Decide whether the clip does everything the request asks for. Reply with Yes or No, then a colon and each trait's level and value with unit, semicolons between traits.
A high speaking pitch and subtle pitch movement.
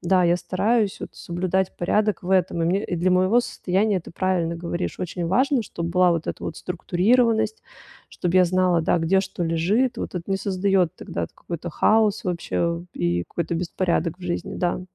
No: medium, 180 Hz; narrow, 2.2 semitones